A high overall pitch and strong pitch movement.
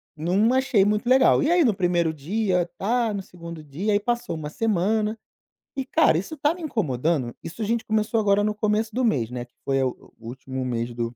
Yes: high, 200 Hz; wide, 6.7 semitones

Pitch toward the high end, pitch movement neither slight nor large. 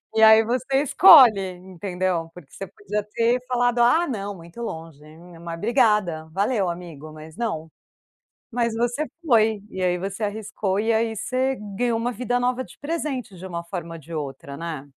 No: high, 205 Hz; wide, 6.1 semitones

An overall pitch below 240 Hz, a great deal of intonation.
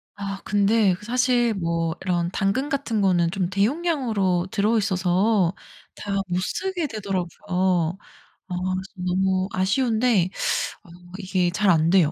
No: high, 190 Hz; average, 3.5 semitones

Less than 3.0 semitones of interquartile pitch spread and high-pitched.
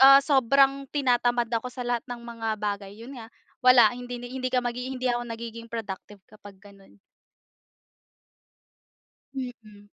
Yes: narrow, 2.4 semitones; high, 240 Hz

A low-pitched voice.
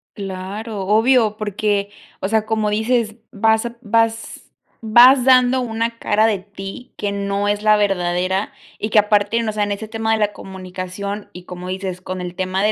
No: high, 210 Hz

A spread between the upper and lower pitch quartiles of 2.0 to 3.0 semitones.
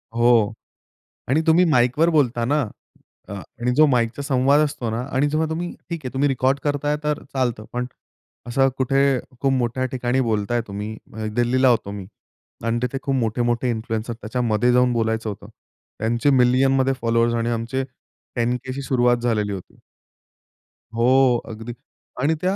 Yes: narrow, 2.6 semitones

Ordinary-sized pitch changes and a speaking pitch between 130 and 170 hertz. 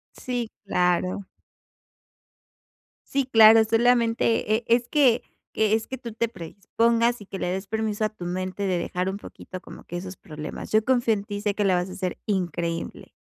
No: average, 3.9 semitones; high, 210 Hz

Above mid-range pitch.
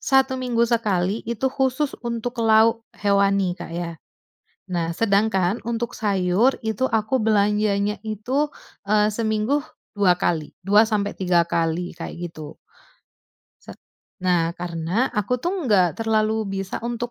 Yes: high, 210 Hz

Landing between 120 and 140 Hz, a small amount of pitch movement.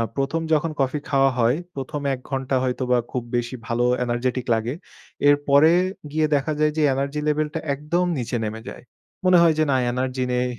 No: low, 135 Hz; average, 3.2 semitones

